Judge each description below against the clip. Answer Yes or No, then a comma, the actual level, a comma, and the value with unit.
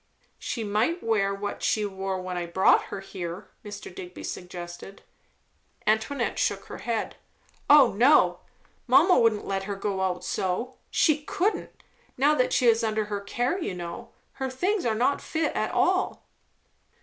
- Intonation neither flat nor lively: Yes, average, 4.8 semitones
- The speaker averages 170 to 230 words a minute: No, average, 160 wpm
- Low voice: No, high, 210 Hz